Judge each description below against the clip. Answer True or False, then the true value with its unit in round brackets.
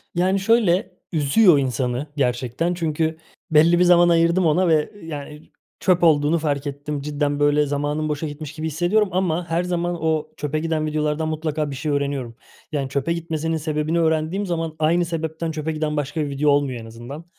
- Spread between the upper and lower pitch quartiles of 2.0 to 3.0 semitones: True (2.4 semitones)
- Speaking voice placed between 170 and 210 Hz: False (155 Hz)